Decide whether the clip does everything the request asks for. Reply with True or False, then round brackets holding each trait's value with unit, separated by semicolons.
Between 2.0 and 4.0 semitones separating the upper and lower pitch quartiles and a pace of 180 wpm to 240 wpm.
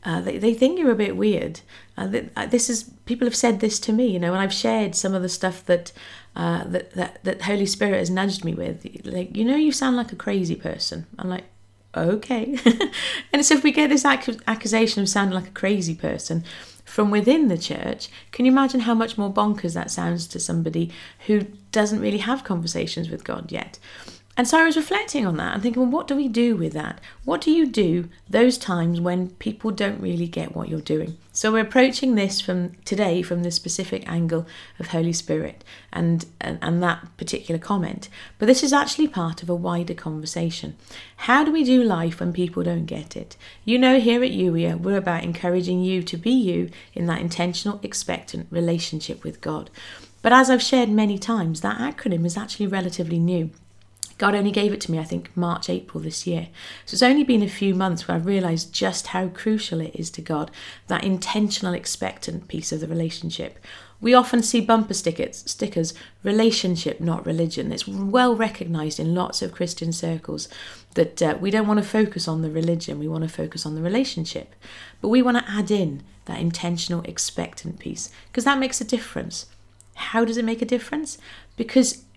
False (5.5 semitones; 200 wpm)